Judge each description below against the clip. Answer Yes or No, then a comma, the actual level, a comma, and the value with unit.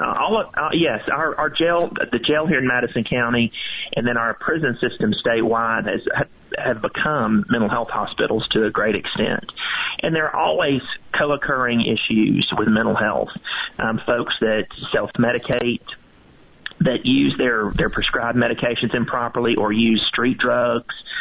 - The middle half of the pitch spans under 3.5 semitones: Yes, narrow, 2.6 semitones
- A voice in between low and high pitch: No, low, 120 Hz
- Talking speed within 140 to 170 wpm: Yes, average, 155 wpm